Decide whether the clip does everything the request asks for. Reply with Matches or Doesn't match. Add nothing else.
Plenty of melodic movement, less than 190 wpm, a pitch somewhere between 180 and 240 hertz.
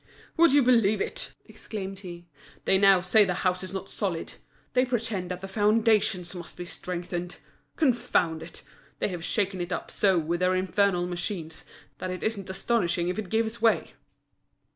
Doesn't match